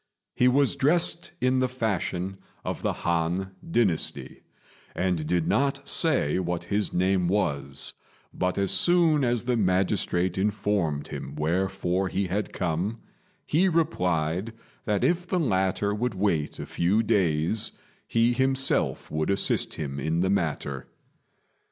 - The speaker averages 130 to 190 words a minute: Yes, slow, 135 wpm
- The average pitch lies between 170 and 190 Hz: No, very low, 95 Hz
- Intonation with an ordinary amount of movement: No, wide, 5.9 semitones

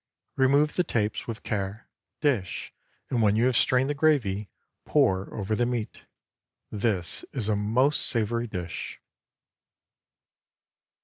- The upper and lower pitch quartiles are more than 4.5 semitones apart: No, average, 4.0 semitones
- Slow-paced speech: Yes, slow, 125 wpm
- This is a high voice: No, low, 110 Hz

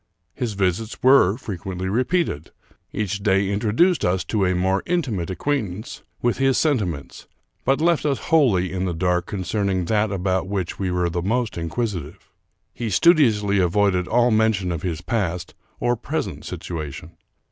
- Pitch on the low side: Yes, low, 100 Hz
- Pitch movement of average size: Yes, average, 4.7 semitones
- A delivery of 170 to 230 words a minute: No, average, 155 wpm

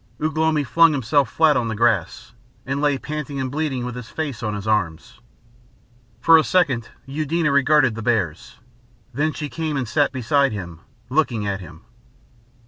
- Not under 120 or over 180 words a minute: Yes, average, 170 wpm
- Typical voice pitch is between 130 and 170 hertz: Yes, low, 135 Hz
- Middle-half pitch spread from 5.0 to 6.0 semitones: Yes, average, 5.3 semitones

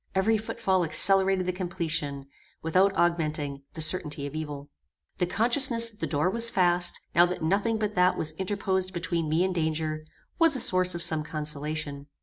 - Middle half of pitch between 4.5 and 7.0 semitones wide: No, average, 3.7 semitones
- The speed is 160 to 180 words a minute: Yes, average, 170 wpm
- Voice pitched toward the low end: No, medium, 175 Hz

